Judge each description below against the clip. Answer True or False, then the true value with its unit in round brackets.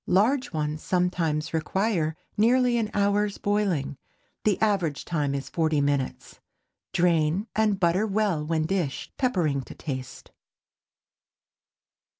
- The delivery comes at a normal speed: False (115 wpm)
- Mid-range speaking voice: True (180 Hz)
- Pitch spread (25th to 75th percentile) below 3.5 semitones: False (5.2 semitones)